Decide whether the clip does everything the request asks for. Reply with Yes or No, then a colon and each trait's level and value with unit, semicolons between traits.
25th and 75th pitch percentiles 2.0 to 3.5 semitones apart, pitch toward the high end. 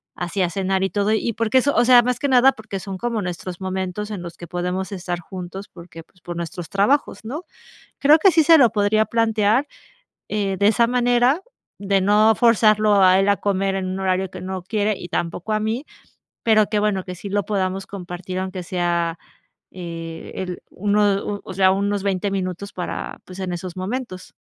Yes: average, 2.8 semitones; high, 195 Hz